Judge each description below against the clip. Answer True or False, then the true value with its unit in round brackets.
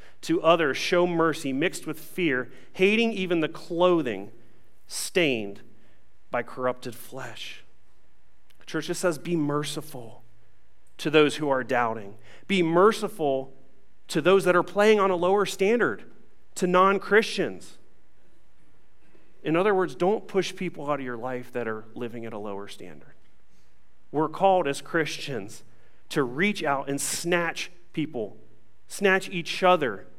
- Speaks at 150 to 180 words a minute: False (140 wpm)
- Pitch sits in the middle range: True (150 Hz)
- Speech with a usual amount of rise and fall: False (7.4 semitones)